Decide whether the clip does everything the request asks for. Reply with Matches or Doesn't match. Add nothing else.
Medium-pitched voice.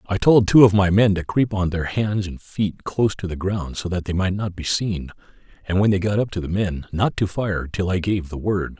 Doesn't match